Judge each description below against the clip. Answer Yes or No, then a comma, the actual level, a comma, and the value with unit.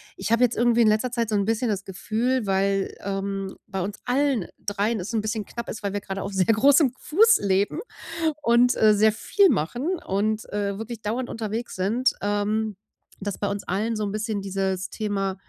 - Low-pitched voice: No, high, 215 Hz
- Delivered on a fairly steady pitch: No, average, 3.0 semitones